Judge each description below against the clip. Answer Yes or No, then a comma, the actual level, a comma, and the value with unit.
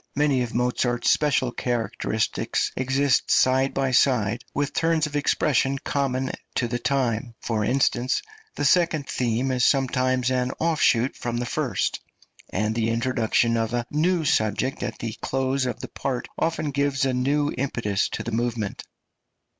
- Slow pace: No, average, 155 wpm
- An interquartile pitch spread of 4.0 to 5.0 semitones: No, average, 2.7 semitones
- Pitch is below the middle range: Yes, low, 130 Hz